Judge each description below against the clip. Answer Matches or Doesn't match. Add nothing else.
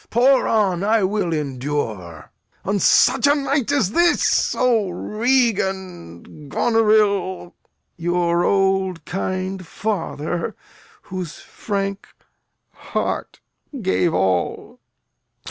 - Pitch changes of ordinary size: Matches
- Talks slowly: Matches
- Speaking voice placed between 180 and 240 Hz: Matches